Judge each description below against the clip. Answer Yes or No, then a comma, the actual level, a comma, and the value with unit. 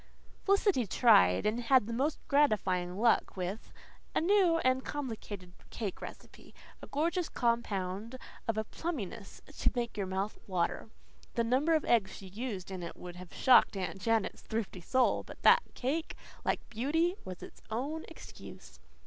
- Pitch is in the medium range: No, high, 230 Hz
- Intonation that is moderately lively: No, wide, 6.3 semitones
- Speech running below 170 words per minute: Yes, average, 155 wpm